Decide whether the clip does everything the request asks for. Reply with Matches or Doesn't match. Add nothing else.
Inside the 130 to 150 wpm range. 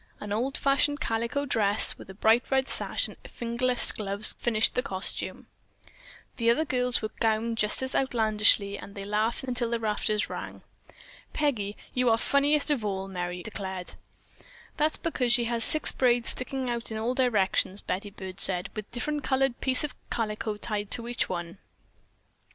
Doesn't match